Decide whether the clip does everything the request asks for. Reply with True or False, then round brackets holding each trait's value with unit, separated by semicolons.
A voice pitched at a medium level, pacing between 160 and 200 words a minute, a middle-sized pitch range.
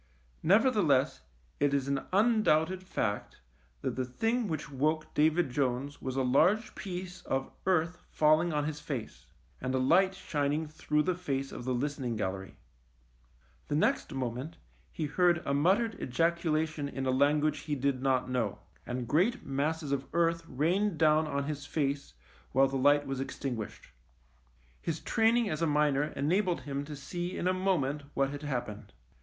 True (150 Hz; 165 wpm; 4.0 semitones)